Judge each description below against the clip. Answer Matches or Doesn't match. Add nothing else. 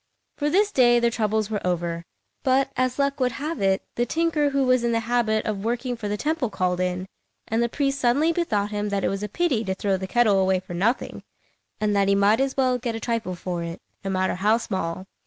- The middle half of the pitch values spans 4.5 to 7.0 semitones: Matches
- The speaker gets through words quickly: Matches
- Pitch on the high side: Matches